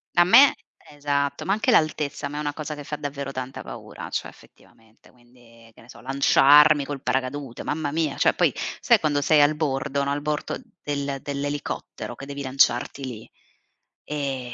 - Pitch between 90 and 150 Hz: Yes, medium, 140 Hz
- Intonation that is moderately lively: No, narrow, 1.8 semitones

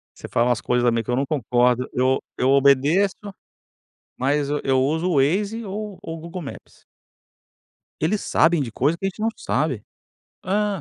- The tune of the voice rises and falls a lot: Yes, wide, 6.3 semitones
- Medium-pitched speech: Yes, medium, 145 Hz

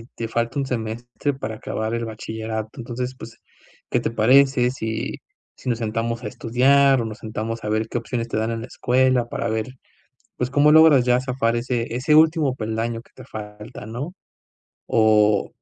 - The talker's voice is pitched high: No, low, 115 Hz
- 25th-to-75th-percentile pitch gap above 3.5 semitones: No, narrow, 2.5 semitones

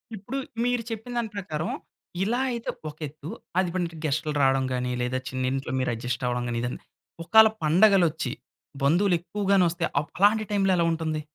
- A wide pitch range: Yes, wide, 6.7 semitones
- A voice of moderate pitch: Yes, medium, 165 Hz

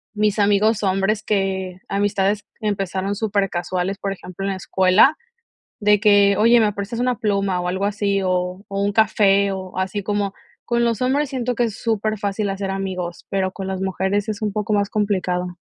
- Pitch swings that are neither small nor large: No, narrow, 1.9 semitones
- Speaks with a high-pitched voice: Yes, high, 200 Hz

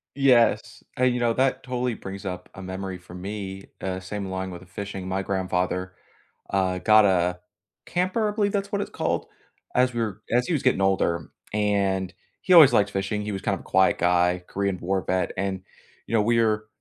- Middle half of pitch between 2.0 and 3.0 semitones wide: No, average, 3.8 semitones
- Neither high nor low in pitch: No, low, 100 Hz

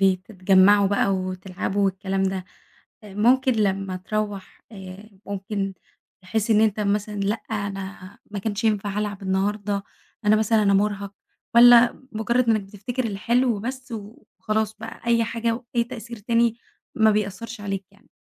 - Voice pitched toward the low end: No, high, 205 Hz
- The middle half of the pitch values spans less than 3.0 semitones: Yes, narrow, 2.4 semitones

